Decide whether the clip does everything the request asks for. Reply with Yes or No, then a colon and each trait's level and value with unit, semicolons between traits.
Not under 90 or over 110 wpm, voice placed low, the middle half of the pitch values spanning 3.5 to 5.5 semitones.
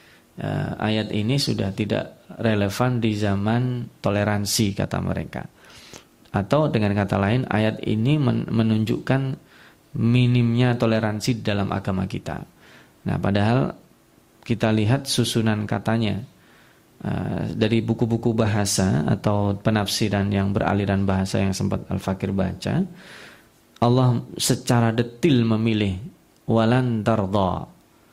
No: average, 100 wpm; low, 110 Hz; average, 3.0 semitones